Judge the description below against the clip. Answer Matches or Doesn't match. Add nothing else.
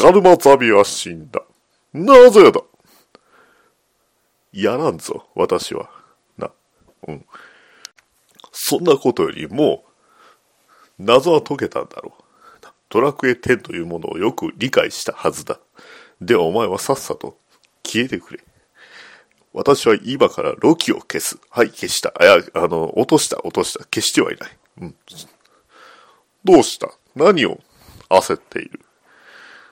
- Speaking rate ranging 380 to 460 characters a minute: Doesn't match